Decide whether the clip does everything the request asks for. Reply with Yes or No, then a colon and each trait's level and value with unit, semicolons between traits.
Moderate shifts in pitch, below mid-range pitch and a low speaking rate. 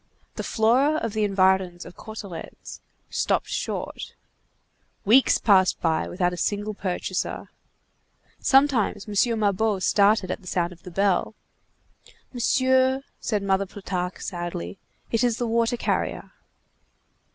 No: average, 3.7 semitones; high, 205 Hz; slow, 125 wpm